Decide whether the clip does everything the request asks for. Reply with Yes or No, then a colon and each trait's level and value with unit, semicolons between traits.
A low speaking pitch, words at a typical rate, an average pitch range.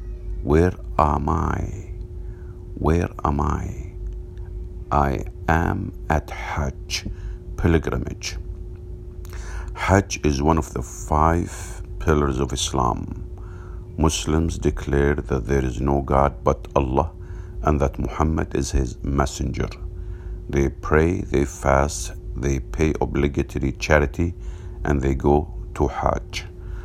No: very low, 85 Hz; slow, 105 wpm; average, 4.0 semitones